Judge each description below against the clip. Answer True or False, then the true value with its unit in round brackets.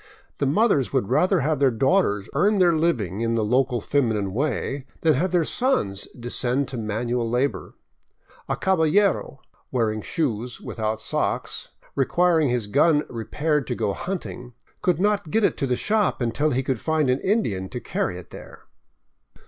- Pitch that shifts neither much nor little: False (6.1 semitones)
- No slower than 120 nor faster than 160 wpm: False (170 wpm)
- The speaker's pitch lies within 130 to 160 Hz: True (135 Hz)